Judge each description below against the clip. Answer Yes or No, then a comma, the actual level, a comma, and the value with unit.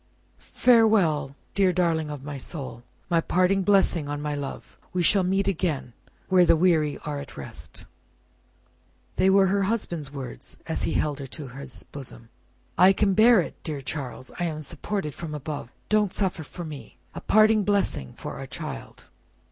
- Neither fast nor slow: Yes, average, 170 wpm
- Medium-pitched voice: Yes, medium, 165 Hz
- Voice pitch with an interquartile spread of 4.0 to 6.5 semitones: Yes, average, 5.2 semitones